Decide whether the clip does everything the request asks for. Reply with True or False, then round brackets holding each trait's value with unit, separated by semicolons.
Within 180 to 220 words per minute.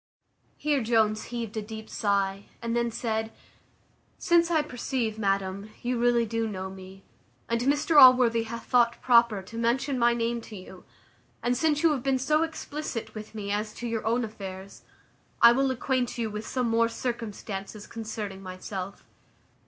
False (165 wpm)